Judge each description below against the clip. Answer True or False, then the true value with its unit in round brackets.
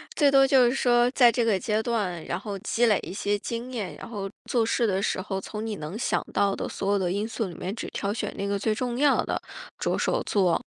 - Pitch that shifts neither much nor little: True (3.4 semitones)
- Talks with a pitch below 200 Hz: False (215 Hz)